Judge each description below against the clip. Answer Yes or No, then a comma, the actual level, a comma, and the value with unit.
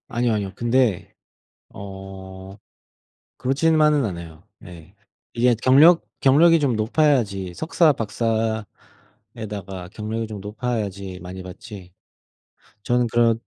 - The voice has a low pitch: Yes, low, 110 Hz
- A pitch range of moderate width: Yes, average, 4.5 semitones